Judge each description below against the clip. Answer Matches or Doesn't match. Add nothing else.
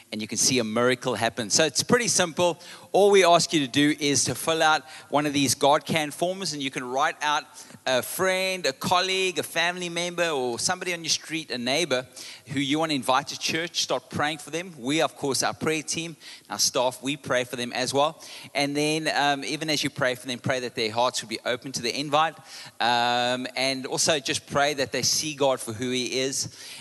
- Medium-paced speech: Doesn't match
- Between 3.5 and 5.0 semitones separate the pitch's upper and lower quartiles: Matches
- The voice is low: Doesn't match